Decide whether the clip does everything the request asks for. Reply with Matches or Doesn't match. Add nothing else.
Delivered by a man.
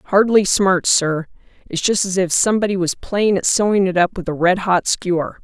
Doesn't match